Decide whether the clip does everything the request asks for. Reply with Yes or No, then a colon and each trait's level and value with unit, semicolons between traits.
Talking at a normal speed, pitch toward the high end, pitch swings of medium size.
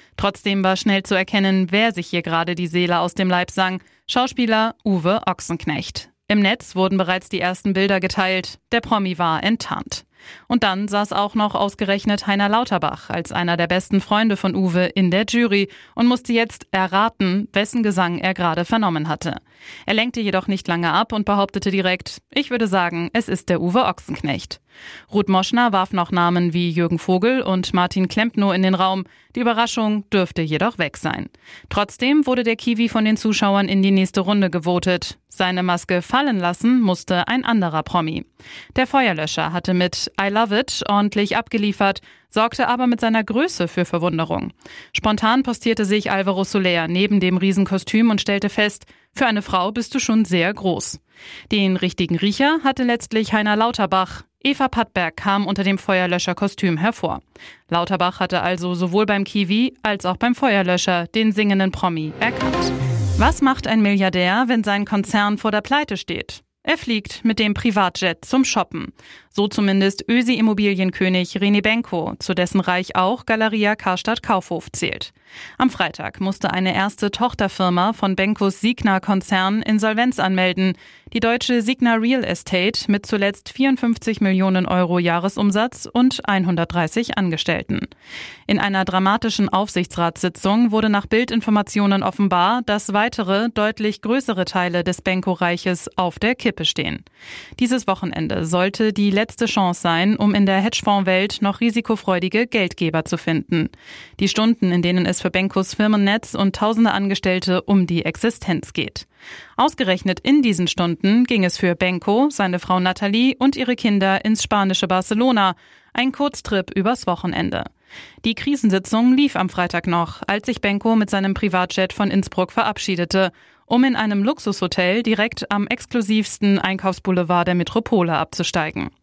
Yes: average, 155 wpm; high, 200 Hz; average, 3.3 semitones